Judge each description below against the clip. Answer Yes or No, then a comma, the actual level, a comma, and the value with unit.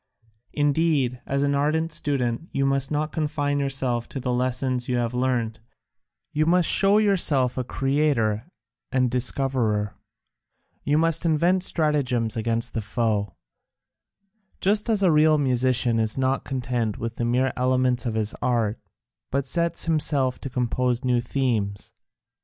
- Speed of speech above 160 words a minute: No, average, 140 wpm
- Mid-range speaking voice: No, low, 130 Hz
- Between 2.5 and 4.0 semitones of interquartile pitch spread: Yes, average, 3.7 semitones